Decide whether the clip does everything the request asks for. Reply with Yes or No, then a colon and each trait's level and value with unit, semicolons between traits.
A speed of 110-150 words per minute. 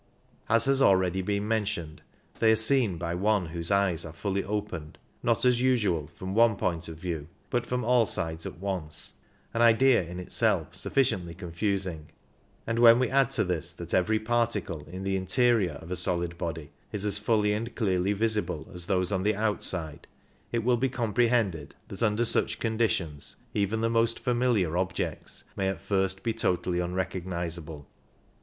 No: average, 175 wpm